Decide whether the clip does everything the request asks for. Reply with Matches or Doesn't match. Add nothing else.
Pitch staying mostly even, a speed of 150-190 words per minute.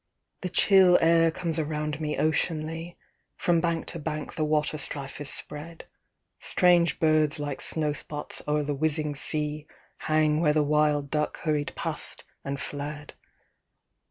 Doesn't match